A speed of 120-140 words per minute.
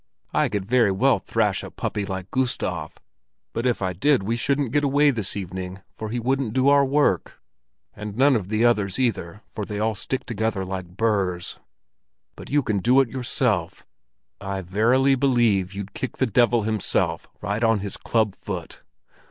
No: average, 175 wpm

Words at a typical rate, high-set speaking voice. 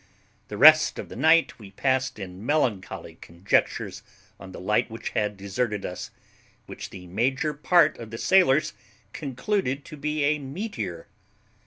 No: average, 150 wpm; low, 130 Hz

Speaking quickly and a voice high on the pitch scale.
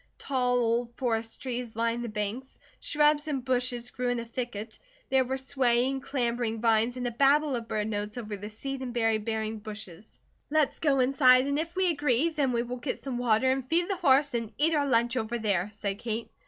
Yes: fast, 210 wpm; high, 245 Hz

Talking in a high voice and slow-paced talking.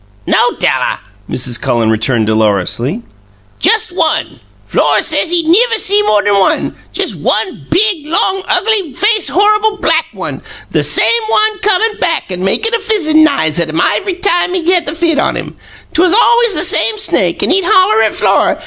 No: very high, 350 Hz; average, 175 wpm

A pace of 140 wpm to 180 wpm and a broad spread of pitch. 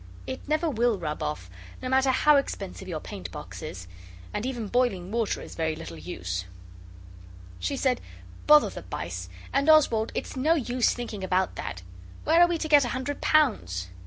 Yes: average, 175 wpm; wide, 8.3 semitones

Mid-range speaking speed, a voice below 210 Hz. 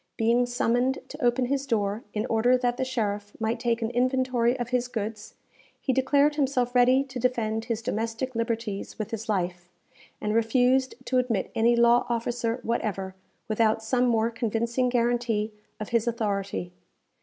No: average, 160 wpm; high, 235 Hz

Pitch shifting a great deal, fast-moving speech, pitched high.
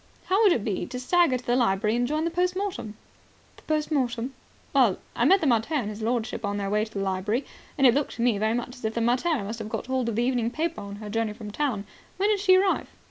Yes: wide, 5.9 semitones; fast, 270 wpm; high, 240 Hz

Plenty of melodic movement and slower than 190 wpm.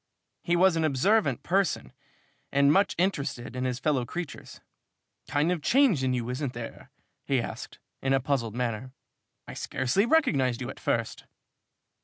Yes: wide, 5.7 semitones; average, 155 wpm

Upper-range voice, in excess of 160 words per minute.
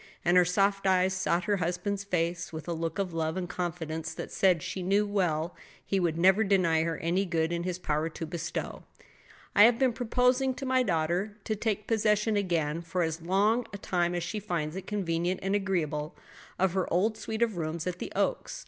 No: medium, 180 Hz; fast, 205 wpm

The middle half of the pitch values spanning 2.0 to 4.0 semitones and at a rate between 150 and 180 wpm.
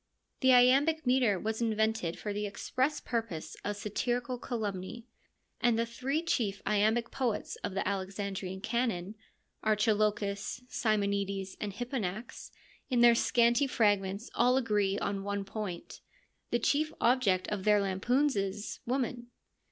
No: average, 3.4 semitones; slow, 135 wpm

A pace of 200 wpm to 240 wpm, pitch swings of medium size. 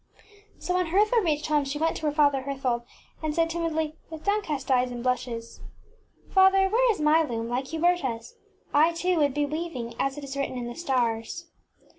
Yes: fast, 205 wpm; average, 4.6 semitones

